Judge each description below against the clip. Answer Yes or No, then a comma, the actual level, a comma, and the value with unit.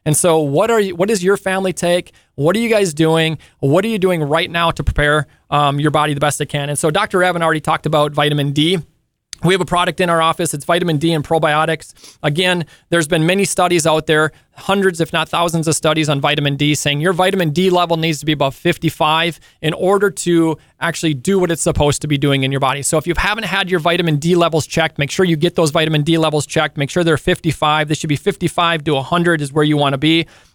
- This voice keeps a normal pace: No, fast, 245 wpm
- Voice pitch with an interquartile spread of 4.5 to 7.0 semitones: No, average, 2.8 semitones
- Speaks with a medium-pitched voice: Yes, medium, 160 Hz